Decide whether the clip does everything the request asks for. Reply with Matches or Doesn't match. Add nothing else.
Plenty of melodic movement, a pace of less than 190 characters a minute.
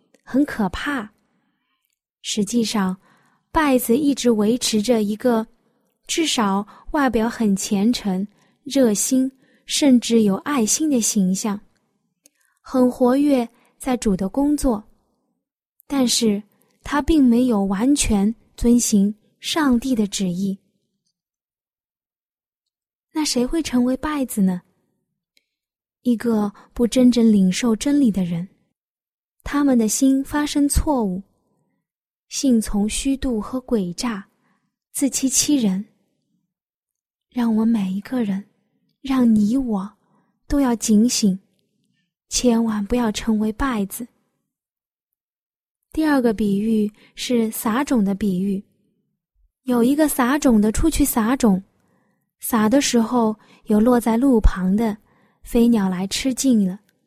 Doesn't match